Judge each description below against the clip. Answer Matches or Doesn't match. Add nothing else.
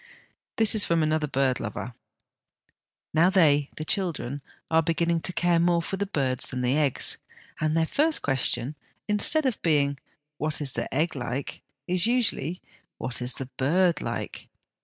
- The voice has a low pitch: Doesn't match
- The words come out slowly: Doesn't match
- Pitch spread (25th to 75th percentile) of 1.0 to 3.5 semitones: Doesn't match